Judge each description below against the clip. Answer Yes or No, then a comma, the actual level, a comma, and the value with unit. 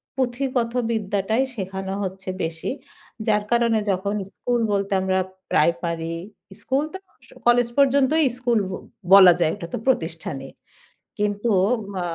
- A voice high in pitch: Yes, high, 205 Hz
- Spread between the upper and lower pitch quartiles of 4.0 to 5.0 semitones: Yes, average, 4.5 semitones